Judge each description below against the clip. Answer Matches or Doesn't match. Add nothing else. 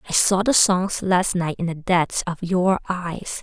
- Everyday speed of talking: Doesn't match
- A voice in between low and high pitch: Matches